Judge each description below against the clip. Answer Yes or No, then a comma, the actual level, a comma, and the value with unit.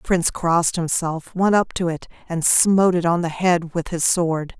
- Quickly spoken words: Yes, fast, 220 wpm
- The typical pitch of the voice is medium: Yes, medium, 170 Hz